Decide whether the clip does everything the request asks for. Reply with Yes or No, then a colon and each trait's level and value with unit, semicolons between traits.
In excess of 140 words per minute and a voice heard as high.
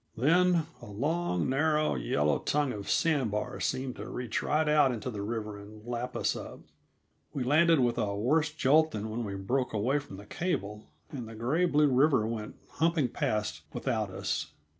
No: average, 185 wpm; low, 125 Hz